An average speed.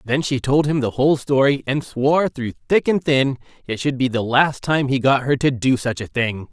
No: fast, 250 wpm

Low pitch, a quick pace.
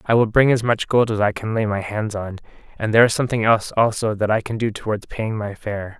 Yes: low, 110 Hz; fast, 270 wpm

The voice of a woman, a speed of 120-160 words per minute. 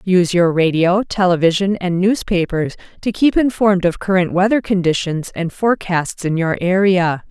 Yes: female; average, 150 wpm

